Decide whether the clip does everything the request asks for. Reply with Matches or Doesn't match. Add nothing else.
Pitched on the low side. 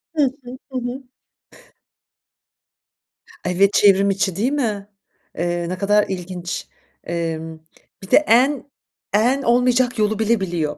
Doesn't match